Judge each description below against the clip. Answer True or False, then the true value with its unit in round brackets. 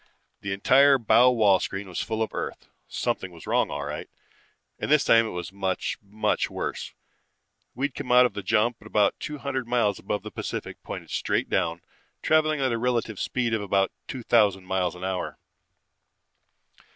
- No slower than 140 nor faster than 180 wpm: True (175 wpm)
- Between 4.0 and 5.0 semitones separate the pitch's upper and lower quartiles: True (4.5 semitones)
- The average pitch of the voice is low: True (110 Hz)